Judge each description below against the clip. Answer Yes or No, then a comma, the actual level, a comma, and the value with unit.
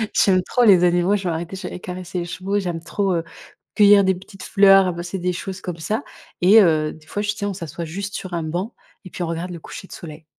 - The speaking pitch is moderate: Yes, medium, 180 Hz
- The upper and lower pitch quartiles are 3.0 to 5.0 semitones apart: No, narrow, 2.4 semitones